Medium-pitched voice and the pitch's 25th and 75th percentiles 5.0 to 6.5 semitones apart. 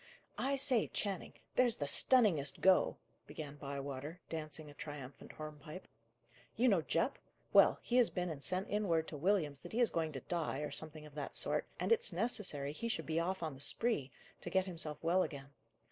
Yes: medium, 160 Hz; average, 5.3 semitones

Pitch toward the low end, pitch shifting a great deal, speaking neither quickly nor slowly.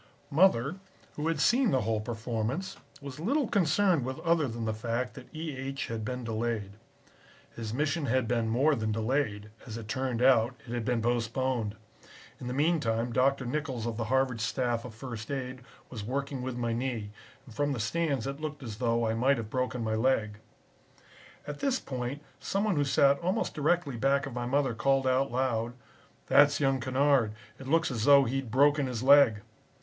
No: low, 130 Hz; average, 3.6 semitones; average, 190 wpm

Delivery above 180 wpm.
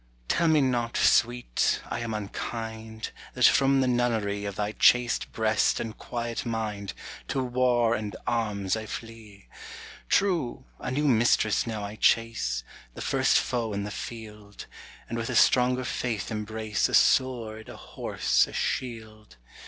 No: average, 150 wpm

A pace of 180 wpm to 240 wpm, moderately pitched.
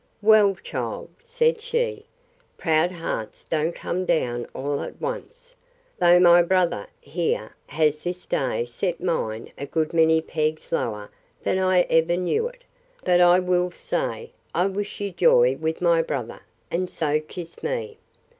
No: average, 150 wpm; medium, 175 Hz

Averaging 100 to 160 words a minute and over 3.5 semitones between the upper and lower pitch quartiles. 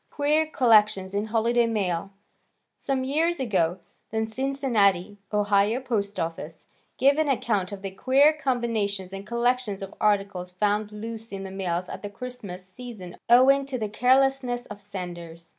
Yes: average, 150 wpm; average, 4.5 semitones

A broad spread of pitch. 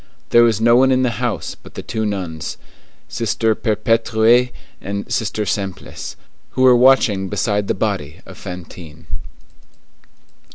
No: average, 3.3 semitones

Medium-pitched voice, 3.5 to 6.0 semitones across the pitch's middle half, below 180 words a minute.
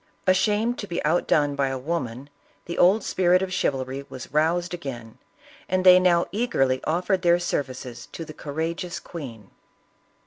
Yes: medium, 170 Hz; average, 5.2 semitones; average, 160 wpm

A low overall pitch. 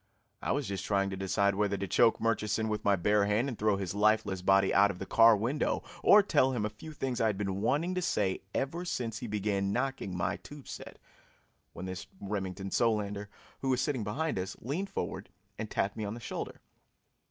Yes: low, 105 Hz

